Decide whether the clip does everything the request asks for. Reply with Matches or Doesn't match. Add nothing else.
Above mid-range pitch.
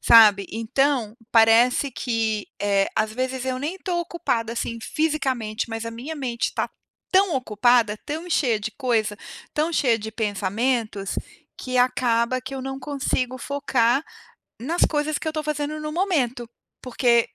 Matches